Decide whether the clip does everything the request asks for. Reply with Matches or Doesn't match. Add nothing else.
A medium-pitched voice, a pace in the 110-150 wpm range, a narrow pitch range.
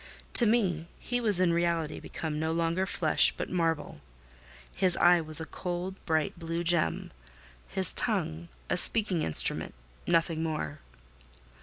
Matches